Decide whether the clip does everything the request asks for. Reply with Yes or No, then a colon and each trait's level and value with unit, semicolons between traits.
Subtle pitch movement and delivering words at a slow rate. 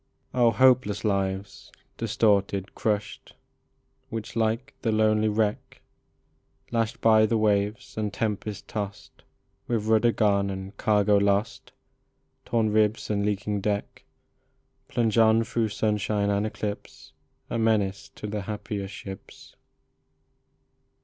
Yes: narrow, 1.6 semitones; slow, 115 wpm